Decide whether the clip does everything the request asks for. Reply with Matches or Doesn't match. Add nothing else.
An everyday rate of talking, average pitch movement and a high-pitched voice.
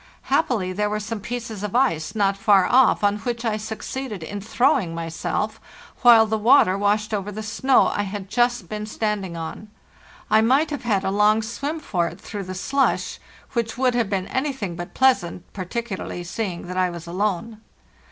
Matches